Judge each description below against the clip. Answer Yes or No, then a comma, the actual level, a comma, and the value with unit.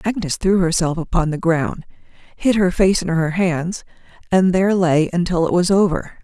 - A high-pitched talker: No, medium, 175 Hz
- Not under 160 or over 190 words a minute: Yes, average, 185 wpm